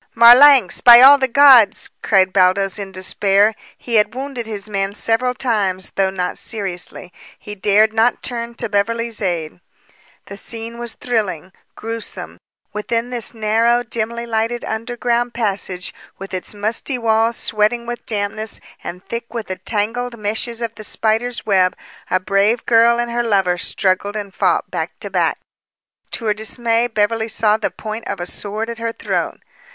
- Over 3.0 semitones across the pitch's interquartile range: No, average, 2.7 semitones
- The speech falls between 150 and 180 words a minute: Yes, average, 160 wpm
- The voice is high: Yes, high, 220 Hz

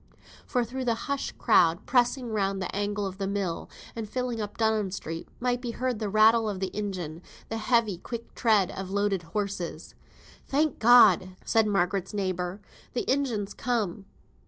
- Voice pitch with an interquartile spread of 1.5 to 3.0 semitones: No, average, 3.5 semitones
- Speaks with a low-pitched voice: No, high, 210 Hz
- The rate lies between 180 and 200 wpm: No, average, 165 wpm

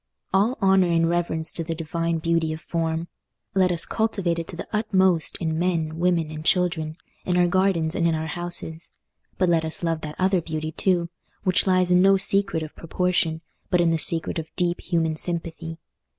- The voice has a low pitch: No, medium, 170 Hz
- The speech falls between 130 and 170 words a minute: No, average, 190 wpm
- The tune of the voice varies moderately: No, narrow, 2.1 semitones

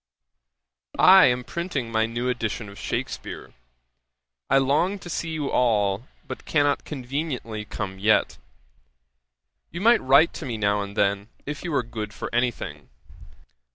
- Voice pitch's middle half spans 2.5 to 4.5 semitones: No, wide, 5.4 semitones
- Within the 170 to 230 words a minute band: No, average, 150 wpm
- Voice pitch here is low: Yes, low, 125 Hz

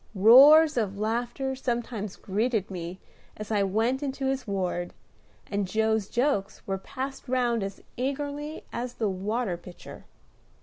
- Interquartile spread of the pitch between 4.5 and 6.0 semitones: Yes, average, 4.9 semitones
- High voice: Yes, high, 225 Hz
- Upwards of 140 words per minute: No, slow, 135 wpm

